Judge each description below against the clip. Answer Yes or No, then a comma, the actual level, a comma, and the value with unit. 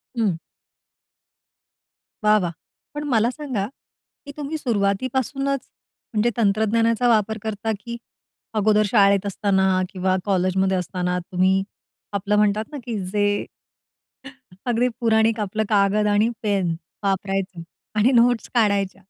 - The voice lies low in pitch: No, high, 210 Hz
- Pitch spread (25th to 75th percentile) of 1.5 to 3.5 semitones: Yes, average, 2.9 semitones